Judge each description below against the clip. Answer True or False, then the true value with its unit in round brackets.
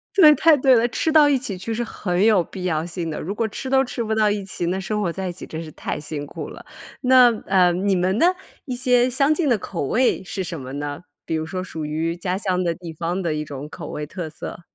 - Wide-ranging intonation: True (6.3 semitones)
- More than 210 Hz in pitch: False (185 Hz)